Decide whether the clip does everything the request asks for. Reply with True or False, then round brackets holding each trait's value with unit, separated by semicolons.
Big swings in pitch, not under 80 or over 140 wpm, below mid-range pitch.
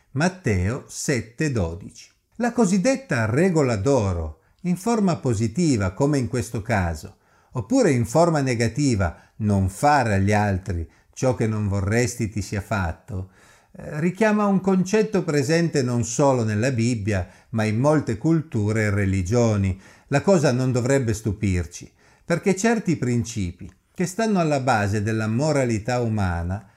True (7.1 semitones; 130 wpm; 120 Hz)